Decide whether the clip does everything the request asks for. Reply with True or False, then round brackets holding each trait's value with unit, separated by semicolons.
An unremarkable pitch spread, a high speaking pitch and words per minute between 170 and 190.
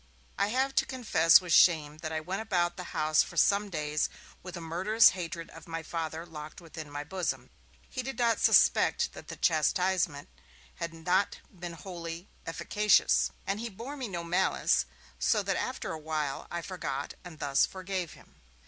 False (3.4 semitones; 170 Hz; 175 wpm)